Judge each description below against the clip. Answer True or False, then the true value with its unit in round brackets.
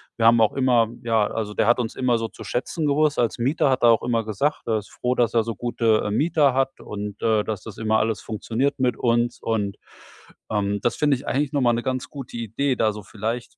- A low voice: True (115 Hz)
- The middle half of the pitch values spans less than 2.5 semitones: False (2.8 semitones)